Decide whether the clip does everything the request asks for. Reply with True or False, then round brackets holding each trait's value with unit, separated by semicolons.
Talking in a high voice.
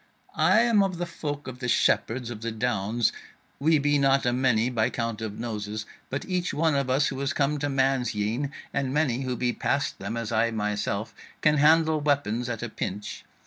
False (130 Hz)